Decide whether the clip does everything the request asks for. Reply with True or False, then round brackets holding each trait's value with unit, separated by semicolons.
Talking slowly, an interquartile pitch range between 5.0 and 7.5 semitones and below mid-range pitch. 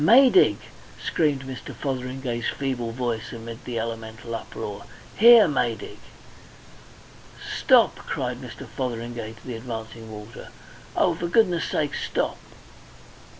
False (110 wpm; 4.0 semitones; 120 Hz)